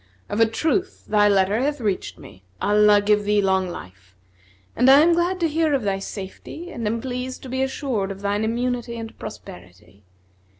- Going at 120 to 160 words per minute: No, average, 185 wpm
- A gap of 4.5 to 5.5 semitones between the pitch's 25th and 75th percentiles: Yes, average, 4.9 semitones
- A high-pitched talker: Yes, high, 220 Hz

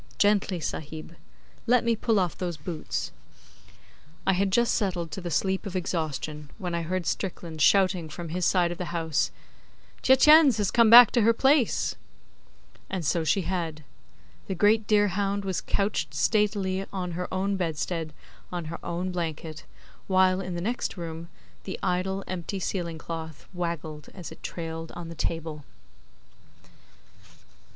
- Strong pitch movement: No, average, 3.2 semitones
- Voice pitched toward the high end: No, medium, 180 Hz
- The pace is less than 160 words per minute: Yes, average, 150 wpm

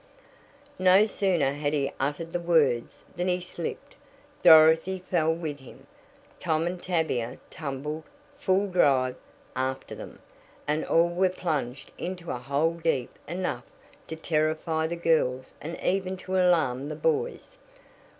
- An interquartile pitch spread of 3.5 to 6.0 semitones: Yes, average, 4.0 semitones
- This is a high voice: No, medium, 160 Hz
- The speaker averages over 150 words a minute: No, slow, 135 wpm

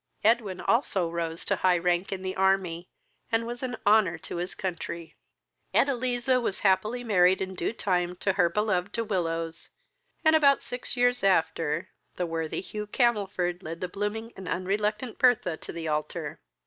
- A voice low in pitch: No, high, 190 Hz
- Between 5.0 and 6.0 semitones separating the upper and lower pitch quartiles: No, average, 4.4 semitones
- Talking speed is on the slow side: No, average, 165 wpm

